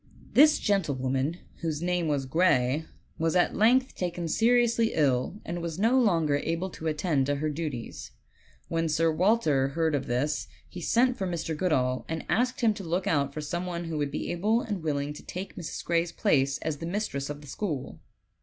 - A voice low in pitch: No, medium, 165 Hz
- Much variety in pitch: No, average, 4.4 semitones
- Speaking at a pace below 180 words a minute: No, average, 190 wpm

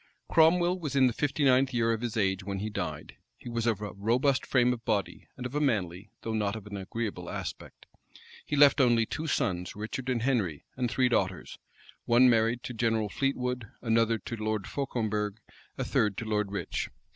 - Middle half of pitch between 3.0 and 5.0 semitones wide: Yes, average, 3.4 semitones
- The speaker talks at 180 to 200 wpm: Yes, average, 195 wpm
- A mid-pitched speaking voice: No, low, 115 Hz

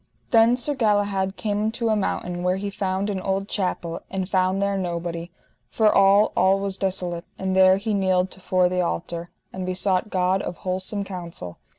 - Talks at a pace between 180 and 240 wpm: Yes, average, 185 wpm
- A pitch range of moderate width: No, narrow, 1.7 semitones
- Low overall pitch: No, high, 190 Hz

